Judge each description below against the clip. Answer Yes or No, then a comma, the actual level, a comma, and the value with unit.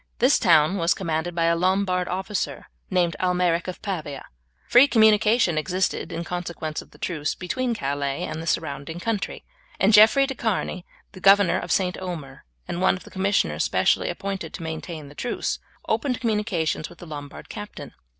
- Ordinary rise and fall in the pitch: Yes, average, 3.9 semitones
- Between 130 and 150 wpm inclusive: No, average, 170 wpm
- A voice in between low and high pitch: Yes, medium, 180 Hz